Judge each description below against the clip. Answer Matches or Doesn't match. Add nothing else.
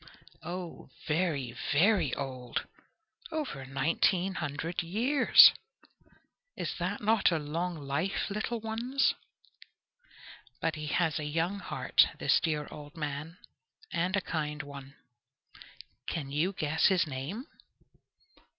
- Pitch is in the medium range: Matches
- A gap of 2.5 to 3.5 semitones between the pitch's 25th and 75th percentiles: Doesn't match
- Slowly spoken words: Matches